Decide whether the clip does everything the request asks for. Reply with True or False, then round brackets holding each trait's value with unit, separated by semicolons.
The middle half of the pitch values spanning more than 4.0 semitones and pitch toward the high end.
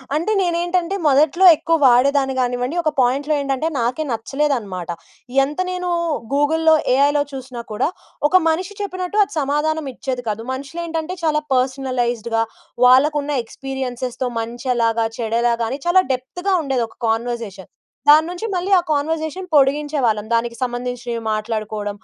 True (4.7 semitones; 270 Hz)